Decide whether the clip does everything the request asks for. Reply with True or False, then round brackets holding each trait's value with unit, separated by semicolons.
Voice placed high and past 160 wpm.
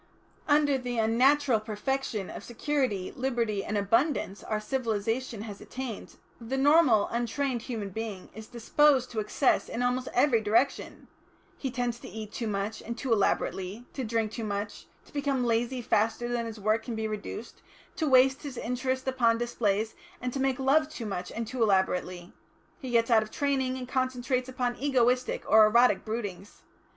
True (235 Hz; 170 wpm)